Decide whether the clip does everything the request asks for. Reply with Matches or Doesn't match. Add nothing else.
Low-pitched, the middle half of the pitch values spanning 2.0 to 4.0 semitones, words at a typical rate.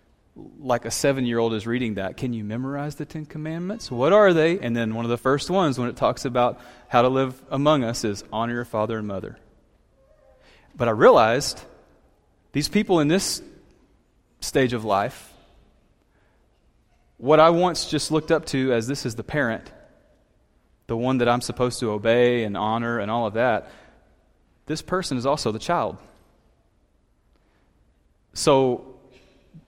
Doesn't match